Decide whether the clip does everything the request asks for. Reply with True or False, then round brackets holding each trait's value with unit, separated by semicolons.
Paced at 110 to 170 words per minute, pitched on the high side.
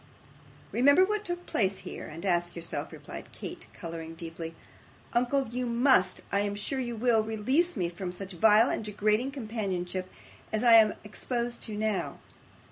True (160 wpm; 215 Hz)